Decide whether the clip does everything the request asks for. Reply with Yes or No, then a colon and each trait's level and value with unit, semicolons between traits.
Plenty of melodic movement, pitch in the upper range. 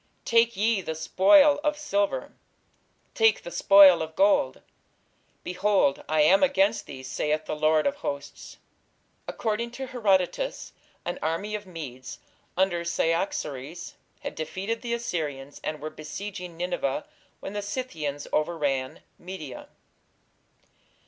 No: wide, 6.1 semitones; medium, 180 Hz